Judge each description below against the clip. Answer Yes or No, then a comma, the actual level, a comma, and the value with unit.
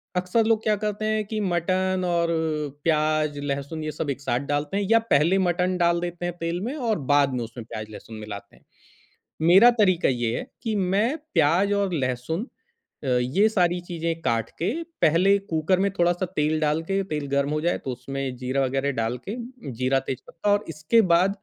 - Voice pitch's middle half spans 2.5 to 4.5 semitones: No, wide, 5.6 semitones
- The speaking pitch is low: No, medium, 165 Hz